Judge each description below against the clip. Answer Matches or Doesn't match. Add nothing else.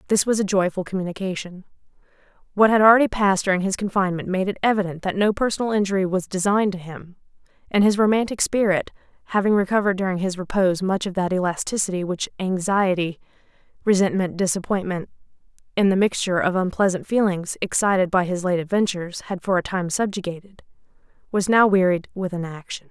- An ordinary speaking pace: Matches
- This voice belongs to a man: Doesn't match